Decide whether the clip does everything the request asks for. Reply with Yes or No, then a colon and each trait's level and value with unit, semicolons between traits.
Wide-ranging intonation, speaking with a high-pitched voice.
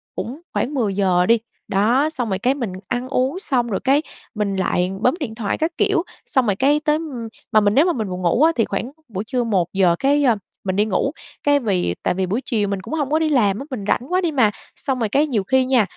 Yes: wide, 5.8 semitones; high, 235 Hz